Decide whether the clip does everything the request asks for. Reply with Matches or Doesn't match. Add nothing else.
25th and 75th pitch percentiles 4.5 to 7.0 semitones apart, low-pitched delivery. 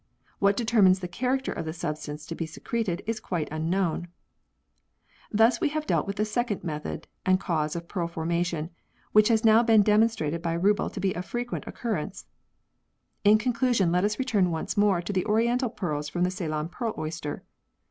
Doesn't match